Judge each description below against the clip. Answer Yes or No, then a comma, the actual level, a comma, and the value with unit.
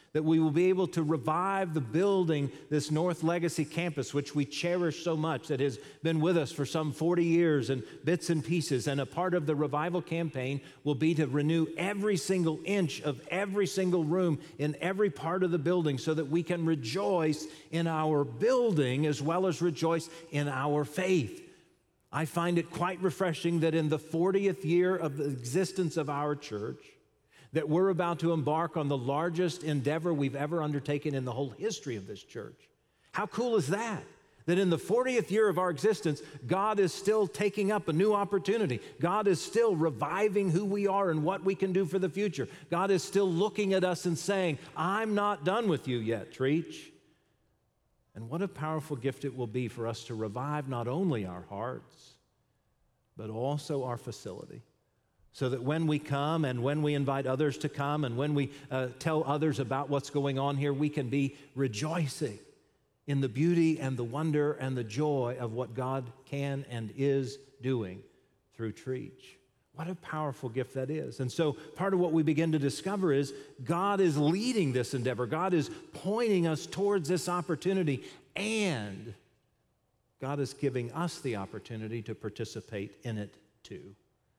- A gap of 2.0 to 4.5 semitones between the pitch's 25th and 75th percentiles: Yes, average, 4.2 semitones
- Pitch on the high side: No, medium, 155 Hz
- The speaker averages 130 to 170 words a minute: No, average, 185 wpm